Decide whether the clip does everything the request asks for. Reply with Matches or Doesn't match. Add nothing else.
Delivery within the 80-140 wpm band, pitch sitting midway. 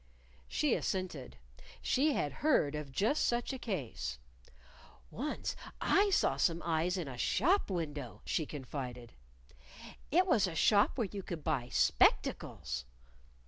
Matches